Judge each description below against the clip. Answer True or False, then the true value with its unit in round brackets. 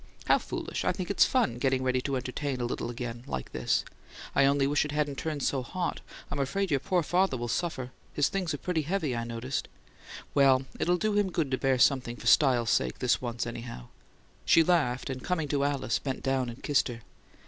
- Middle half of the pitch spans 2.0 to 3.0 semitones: False (3.9 semitones)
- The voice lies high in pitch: False (135 Hz)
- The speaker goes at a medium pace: False (210 wpm)